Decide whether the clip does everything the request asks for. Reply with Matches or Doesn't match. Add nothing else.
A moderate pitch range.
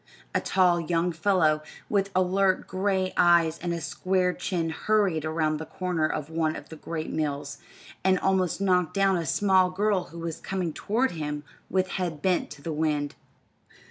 Matches